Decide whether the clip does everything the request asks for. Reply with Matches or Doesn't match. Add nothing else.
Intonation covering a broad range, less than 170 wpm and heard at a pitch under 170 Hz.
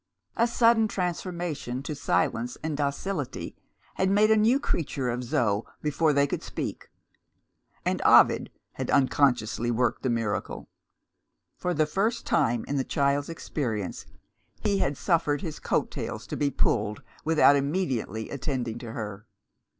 Matches